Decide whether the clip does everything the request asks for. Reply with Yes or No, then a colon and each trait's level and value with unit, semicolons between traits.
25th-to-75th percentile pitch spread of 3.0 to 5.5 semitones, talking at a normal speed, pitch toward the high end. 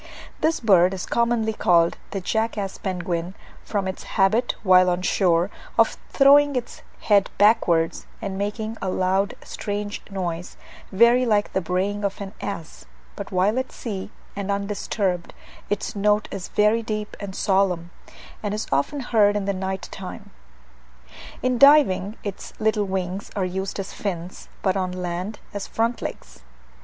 No: narrow, 2.6 semitones; average, 155 wpm; high, 200 Hz